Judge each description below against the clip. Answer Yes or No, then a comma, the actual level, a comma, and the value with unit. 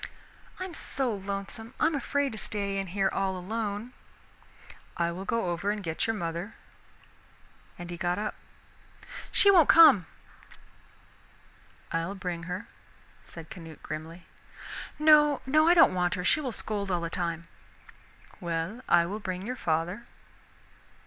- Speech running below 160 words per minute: Yes, average, 140 wpm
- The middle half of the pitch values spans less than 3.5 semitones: No, average, 5.0 semitones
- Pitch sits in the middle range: No, high, 195 Hz